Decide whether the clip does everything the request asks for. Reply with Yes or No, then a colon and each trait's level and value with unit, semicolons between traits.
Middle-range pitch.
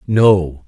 No: low, 105 Hz